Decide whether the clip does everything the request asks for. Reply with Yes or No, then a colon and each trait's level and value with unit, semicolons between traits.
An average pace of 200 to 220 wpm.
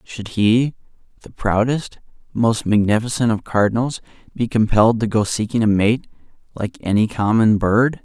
No: average, 140 wpm